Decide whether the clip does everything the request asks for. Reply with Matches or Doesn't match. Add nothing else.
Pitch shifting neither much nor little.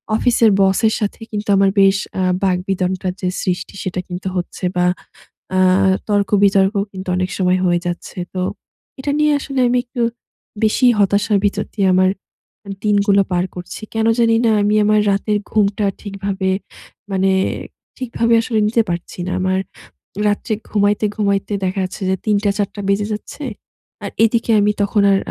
Doesn't match